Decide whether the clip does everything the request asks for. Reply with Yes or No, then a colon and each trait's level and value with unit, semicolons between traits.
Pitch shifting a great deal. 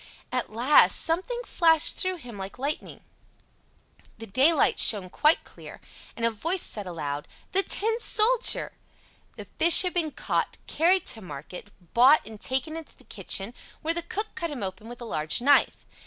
Yes: wide, 7.8 semitones